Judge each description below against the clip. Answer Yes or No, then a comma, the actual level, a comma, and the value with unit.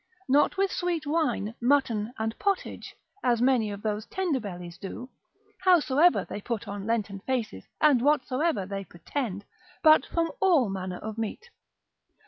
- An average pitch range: No, wide, 7.0 semitones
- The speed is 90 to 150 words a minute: Yes, average, 145 wpm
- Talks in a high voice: Yes, high, 245 Hz